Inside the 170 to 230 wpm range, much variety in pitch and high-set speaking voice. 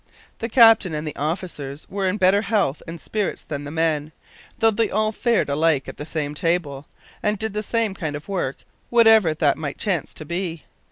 No: average, 190 wpm; wide, 5.9 semitones; medium, 170 Hz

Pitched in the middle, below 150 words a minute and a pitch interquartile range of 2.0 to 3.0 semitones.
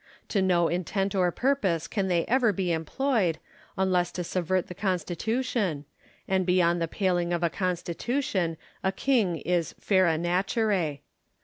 Yes: medium, 180 Hz; average, 140 wpm; narrow, 2.5 semitones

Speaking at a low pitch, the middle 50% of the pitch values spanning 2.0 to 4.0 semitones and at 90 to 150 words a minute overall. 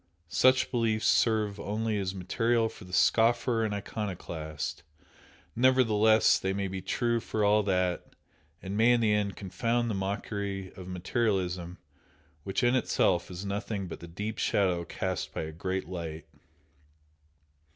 Yes: low, 100 Hz; average, 3.4 semitones; average, 145 wpm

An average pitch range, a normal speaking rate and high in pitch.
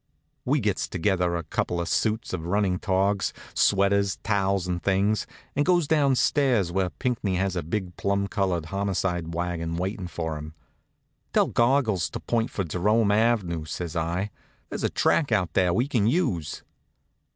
No: average, 3.7 semitones; average, 155 wpm; very low, 95 Hz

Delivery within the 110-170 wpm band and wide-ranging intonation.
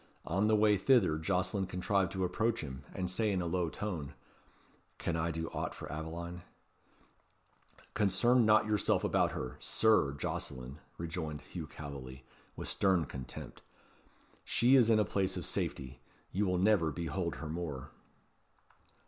No: average, 150 wpm; average, 4.5 semitones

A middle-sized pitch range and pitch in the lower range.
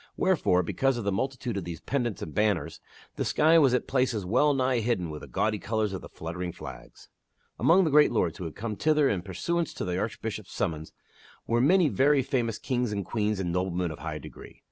No: wide, 6.5 semitones; low, 110 Hz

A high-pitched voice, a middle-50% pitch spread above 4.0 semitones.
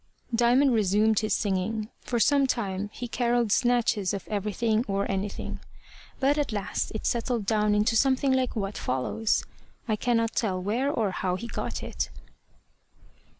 No: high, 220 Hz; average, 3.0 semitones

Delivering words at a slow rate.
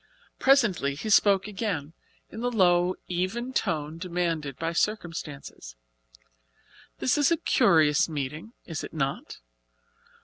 Yes: slow, 115 wpm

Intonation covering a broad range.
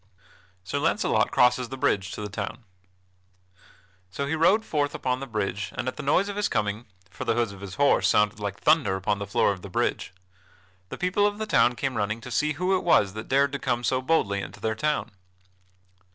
Yes: wide, 6.1 semitones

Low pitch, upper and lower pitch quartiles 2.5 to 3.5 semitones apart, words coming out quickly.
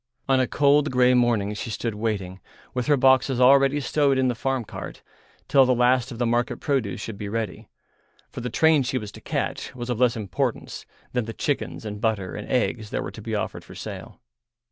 Yes: low, 125 Hz; average, 3.1 semitones; fast, 210 wpm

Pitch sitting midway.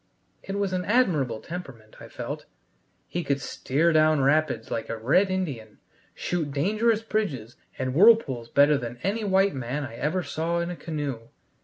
Yes: medium, 155 Hz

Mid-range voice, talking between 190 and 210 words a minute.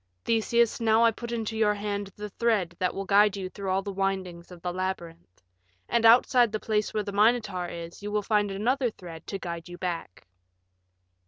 No: high, 200 Hz; average, 195 wpm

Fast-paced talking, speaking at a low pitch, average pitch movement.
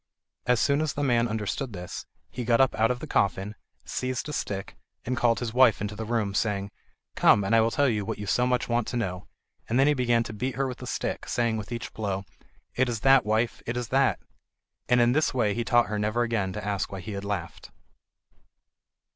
Yes: fast, 230 wpm; low, 115 Hz; average, 3.1 semitones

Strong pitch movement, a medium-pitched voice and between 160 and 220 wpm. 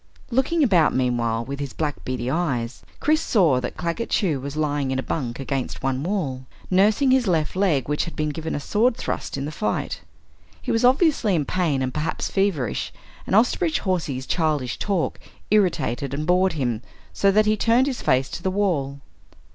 Yes: wide, 7.2 semitones; medium, 160 Hz; average, 185 wpm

